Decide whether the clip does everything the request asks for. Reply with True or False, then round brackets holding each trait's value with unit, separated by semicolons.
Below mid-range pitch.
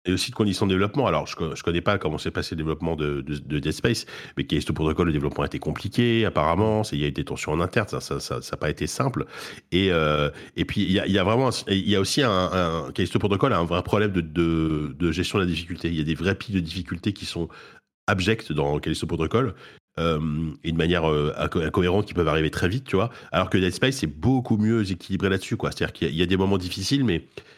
True (90 Hz)